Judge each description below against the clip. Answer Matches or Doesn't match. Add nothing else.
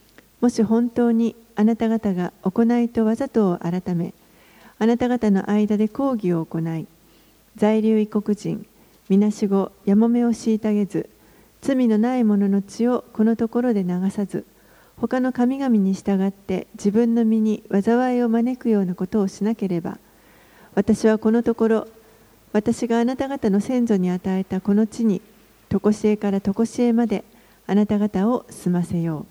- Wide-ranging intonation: Doesn't match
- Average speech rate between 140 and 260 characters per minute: Doesn't match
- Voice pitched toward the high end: Matches